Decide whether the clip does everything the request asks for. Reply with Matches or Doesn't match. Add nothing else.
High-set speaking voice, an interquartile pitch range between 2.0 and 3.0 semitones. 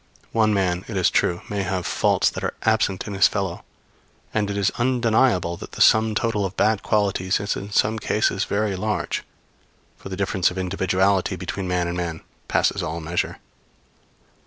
Doesn't match